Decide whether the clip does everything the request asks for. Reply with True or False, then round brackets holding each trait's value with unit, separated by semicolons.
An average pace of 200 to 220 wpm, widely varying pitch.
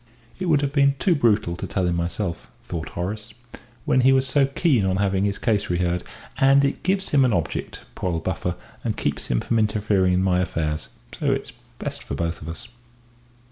True (205 wpm; 7.3 semitones)